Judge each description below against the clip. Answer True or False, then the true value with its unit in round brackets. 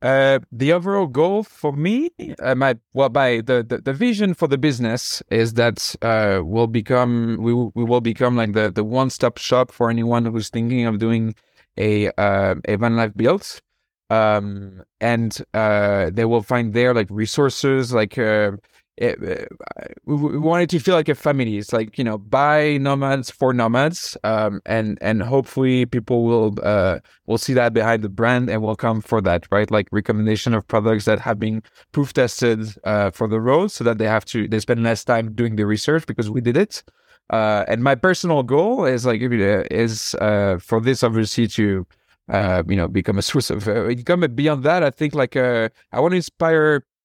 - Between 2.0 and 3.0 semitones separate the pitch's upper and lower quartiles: False (3.5 semitones)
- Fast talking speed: False (195 wpm)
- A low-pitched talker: True (115 Hz)